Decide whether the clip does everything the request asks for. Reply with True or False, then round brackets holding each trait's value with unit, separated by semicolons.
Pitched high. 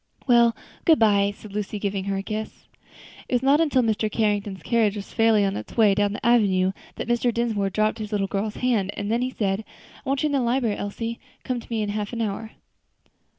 True (215 Hz)